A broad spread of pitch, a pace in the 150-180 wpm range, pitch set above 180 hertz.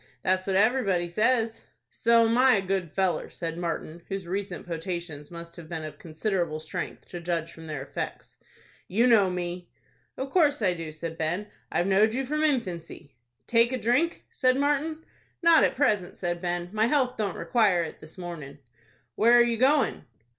Yes: wide, 5.9 semitones; average, 175 wpm; high, 190 Hz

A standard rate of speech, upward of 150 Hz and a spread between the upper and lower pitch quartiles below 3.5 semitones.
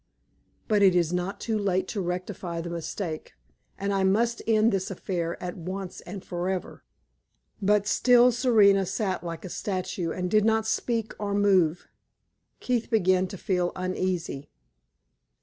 Yes: average, 150 wpm; high, 190 Hz; average, 2.7 semitones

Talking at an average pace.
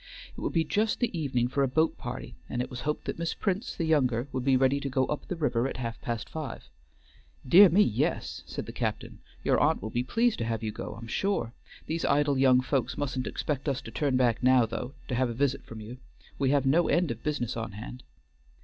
No: fast, 240 wpm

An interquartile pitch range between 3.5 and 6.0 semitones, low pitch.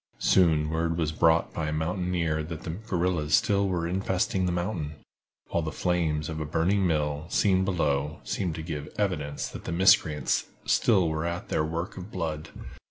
No: average, 2.9 semitones; very low, 85 Hz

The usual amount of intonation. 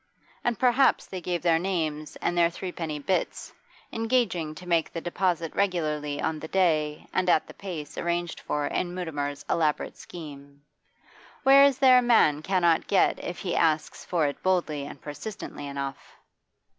Yes: average, 3.7 semitones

